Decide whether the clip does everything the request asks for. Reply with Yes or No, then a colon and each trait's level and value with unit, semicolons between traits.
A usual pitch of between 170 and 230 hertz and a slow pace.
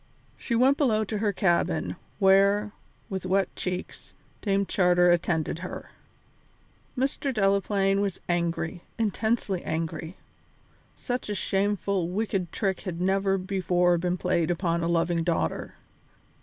Yes: high, 190 Hz; slow, 125 wpm